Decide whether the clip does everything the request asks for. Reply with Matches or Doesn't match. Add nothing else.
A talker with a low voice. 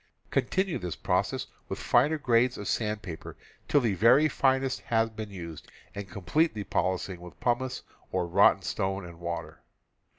Matches